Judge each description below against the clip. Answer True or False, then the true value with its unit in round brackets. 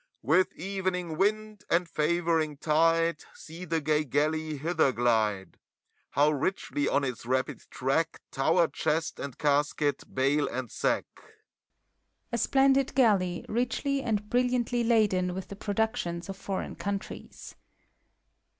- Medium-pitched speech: True (170 Hz)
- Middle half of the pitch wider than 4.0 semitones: True (5.4 semitones)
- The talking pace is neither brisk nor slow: False (125 wpm)